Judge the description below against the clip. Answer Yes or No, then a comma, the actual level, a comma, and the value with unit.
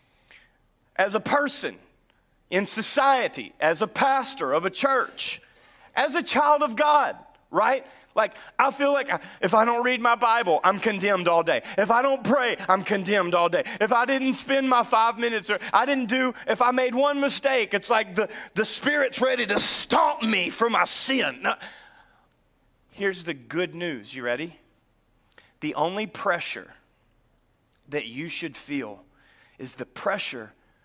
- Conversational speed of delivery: Yes, average, 165 wpm